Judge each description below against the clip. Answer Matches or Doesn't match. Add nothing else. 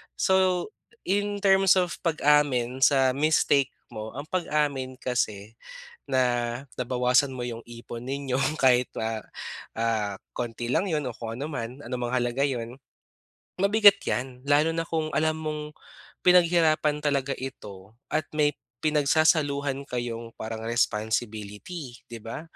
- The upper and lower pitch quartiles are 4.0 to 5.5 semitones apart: Matches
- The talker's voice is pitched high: Doesn't match